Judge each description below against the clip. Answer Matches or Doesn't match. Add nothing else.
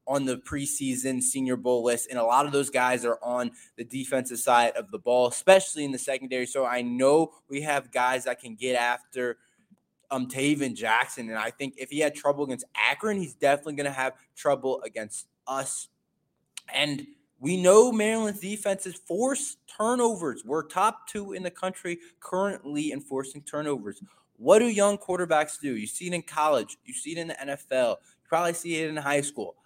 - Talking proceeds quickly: Doesn't match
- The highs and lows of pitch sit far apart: Matches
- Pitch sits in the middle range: Matches